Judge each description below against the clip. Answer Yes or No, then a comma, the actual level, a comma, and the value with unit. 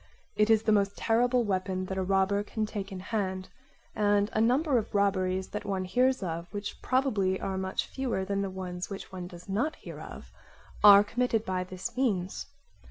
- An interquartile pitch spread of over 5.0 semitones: No, average, 2.8 semitones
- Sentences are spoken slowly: No, average, 190 wpm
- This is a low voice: No, high, 200 Hz